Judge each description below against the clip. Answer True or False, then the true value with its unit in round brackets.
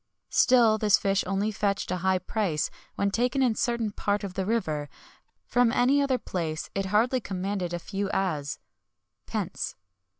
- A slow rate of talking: False (165 wpm)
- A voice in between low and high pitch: False (200 Hz)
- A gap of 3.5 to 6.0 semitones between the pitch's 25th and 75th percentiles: True (3.8 semitones)